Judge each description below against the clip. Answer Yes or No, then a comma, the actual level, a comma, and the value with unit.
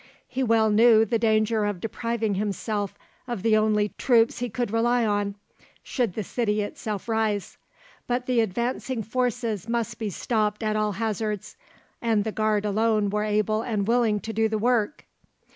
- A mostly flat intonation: Yes, narrow, 1.9 semitones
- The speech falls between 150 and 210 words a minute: Yes, average, 165 wpm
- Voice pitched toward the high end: Yes, high, 220 Hz